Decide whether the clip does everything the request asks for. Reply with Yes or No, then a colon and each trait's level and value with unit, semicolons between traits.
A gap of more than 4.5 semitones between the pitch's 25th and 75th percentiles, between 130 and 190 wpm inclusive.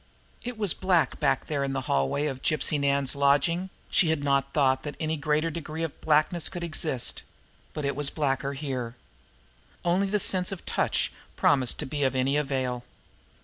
No: average, 3.0 semitones; average, 180 wpm